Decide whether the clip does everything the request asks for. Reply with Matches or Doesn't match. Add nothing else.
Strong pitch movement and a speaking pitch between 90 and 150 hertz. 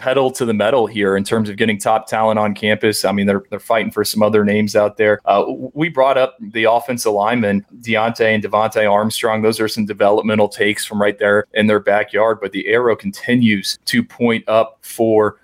Doesn't match